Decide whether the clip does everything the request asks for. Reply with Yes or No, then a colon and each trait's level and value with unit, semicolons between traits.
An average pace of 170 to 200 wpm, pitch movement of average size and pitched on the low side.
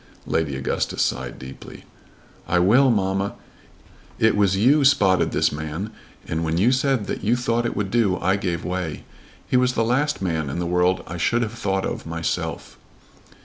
No: average, 180 wpm; wide, 5.7 semitones; very low, 95 Hz